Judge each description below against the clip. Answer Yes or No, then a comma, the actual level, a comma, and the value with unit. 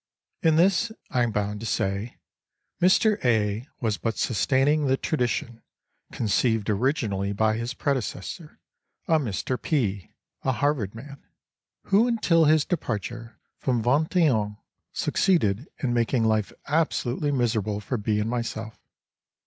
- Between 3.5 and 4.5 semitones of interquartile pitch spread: No, average, 5.3 semitones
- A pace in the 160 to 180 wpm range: No, slow, 135 wpm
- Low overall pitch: Yes, low, 120 Hz